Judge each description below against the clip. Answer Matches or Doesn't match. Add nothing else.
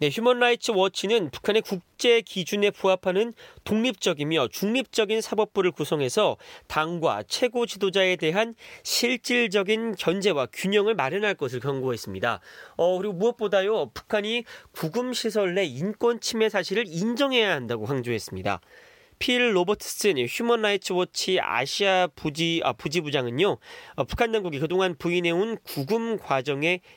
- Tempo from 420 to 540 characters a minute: Doesn't match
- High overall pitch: Matches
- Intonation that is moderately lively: Matches